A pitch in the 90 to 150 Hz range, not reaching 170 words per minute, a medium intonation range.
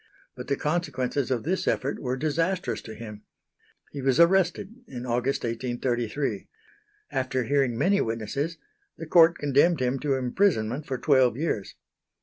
Yes: low, 135 Hz; average, 140 wpm; average, 4.8 semitones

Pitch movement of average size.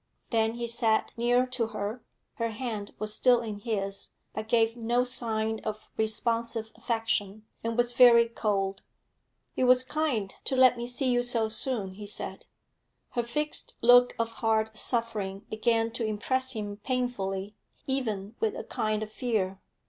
No: narrow, 2.2 semitones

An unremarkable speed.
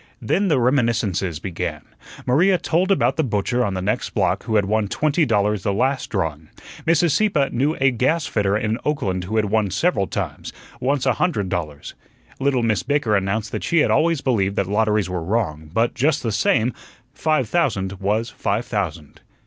Yes: average, 180 wpm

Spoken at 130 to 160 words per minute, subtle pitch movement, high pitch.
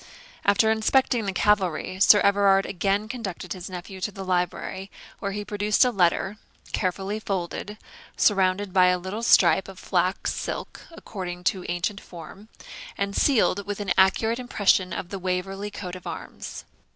Yes: average, 155 wpm; narrow, 2.1 semitones; high, 195 Hz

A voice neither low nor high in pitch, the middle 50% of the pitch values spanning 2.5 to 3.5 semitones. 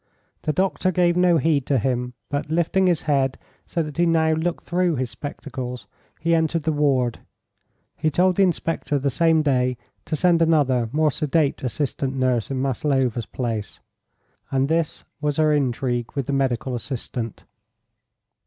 No: medium, 145 Hz; average, 4.1 semitones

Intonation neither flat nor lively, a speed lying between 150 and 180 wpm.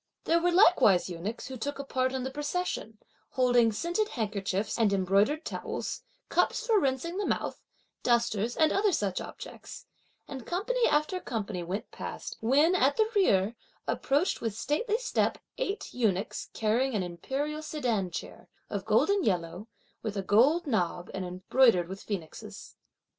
No: wide, 7.7 semitones; average, 155 wpm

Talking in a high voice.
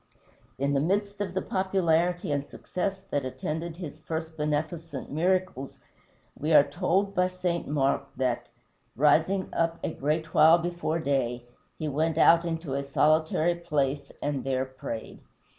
No: medium, 160 Hz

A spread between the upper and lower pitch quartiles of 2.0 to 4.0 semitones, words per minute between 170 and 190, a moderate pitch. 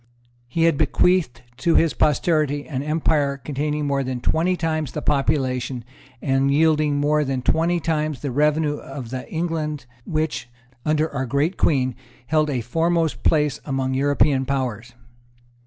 No: average, 2.9 semitones; average, 145 wpm; medium, 145 Hz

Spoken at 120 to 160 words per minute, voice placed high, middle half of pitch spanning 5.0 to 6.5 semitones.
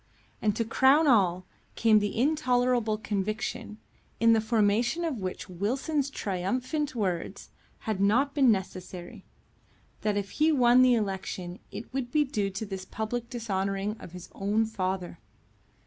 No: average, 145 wpm; high, 220 Hz; average, 4.3 semitones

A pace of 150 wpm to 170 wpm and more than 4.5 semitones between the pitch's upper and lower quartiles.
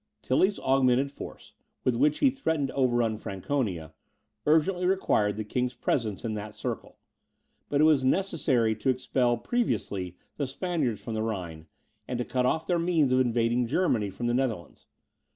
Yes: average, 165 wpm; average, 5.2 semitones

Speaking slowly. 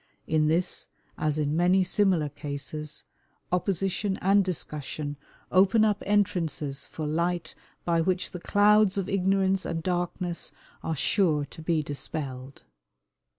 Yes: slow, 125 wpm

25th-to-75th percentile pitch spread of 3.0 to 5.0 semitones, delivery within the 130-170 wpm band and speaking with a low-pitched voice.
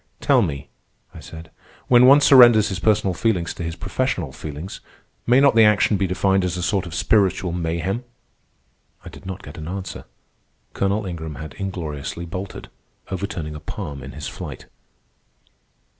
Yes: average, 3.8 semitones; average, 160 wpm; very low, 95 Hz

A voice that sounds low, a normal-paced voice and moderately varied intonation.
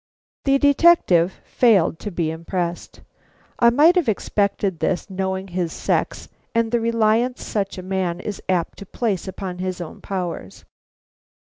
No: high, 190 Hz; average, 145 wpm; average, 4.4 semitones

